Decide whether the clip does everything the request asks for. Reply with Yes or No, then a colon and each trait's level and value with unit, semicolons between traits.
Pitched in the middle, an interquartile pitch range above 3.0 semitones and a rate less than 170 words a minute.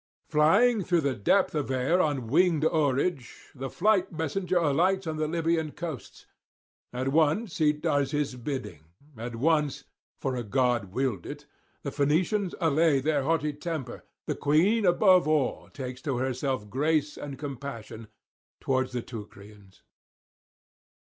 Yes: medium, 145 Hz; average, 4.1 semitones; average, 140 wpm